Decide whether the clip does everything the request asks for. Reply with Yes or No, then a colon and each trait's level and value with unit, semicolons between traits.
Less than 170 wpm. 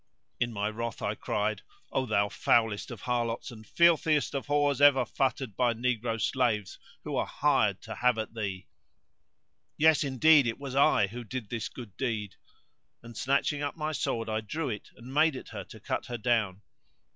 No: average, 180 wpm